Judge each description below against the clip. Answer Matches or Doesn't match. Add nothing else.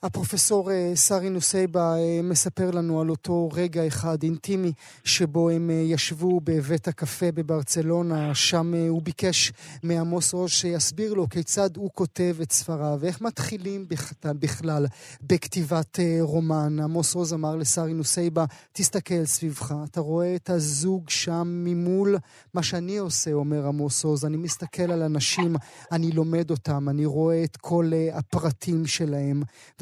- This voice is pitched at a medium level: Matches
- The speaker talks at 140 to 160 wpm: Doesn't match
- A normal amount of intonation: Doesn't match